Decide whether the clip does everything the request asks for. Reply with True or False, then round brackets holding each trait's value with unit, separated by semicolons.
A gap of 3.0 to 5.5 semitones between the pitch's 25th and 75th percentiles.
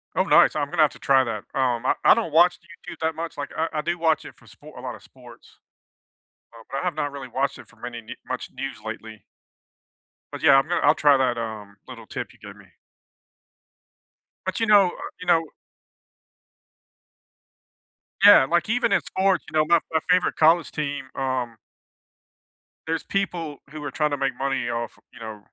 True (4.9 semitones)